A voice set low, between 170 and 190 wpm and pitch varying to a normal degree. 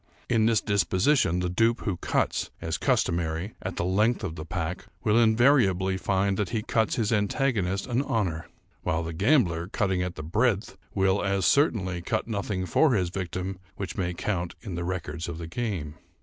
Yes: very low, 95 Hz; average, 180 wpm; average, 4.1 semitones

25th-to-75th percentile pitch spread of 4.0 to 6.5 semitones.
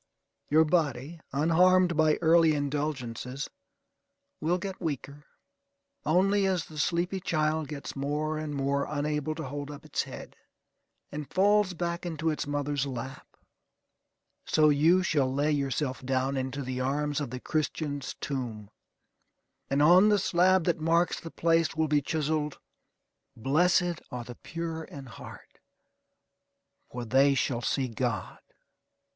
No: average, 3.3 semitones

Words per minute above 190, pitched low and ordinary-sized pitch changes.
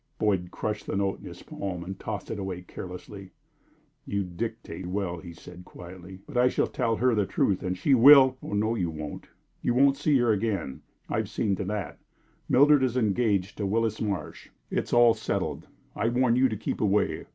Yes: average, 200 wpm; low, 105 Hz; average, 4.2 semitones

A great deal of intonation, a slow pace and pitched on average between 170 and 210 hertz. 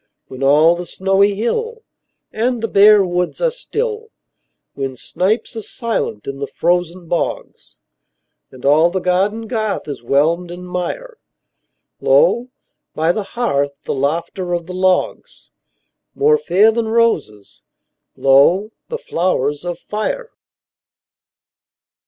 Yes: wide, 5.9 semitones; slow, 125 wpm; medium, 185 Hz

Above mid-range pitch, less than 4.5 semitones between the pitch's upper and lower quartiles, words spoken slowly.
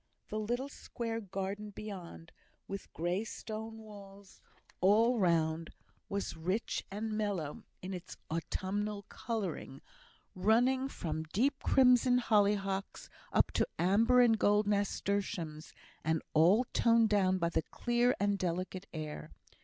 Yes: high, 200 Hz; average, 3.5 semitones; slow, 120 wpm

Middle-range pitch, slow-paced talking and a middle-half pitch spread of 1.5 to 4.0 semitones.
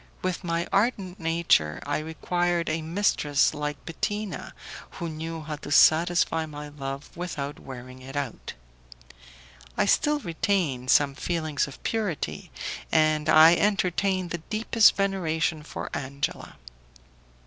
Yes: medium, 160 Hz; slow, 125 wpm; average, 3.5 semitones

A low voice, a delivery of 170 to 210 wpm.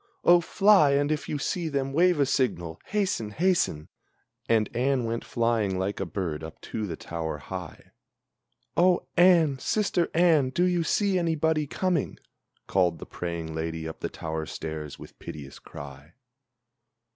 No: low, 125 Hz; average, 155 wpm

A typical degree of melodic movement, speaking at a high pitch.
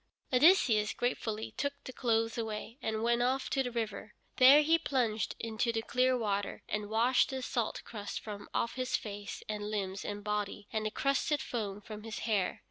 Yes: average, 3.2 semitones; high, 225 Hz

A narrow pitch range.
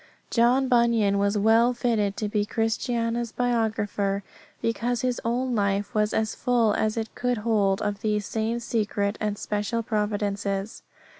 Yes: narrow, 2.3 semitones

